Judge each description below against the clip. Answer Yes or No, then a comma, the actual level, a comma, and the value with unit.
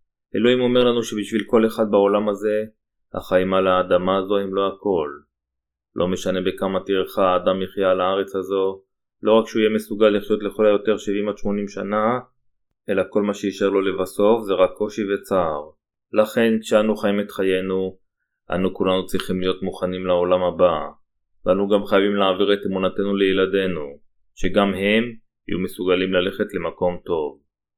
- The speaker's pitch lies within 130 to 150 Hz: No, low, 100 Hz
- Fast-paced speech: Yes, fast, 155 wpm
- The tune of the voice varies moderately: No, narrow, 2.0 semitones